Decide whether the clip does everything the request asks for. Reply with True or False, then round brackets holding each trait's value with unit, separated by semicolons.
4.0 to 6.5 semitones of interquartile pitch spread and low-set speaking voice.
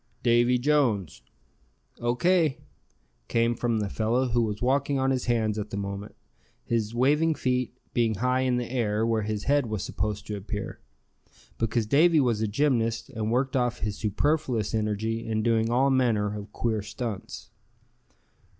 False (3.0 semitones; 115 Hz)